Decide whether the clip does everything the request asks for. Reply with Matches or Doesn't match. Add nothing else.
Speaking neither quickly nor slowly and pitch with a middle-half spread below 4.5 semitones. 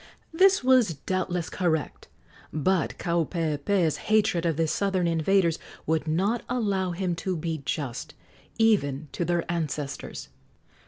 Doesn't match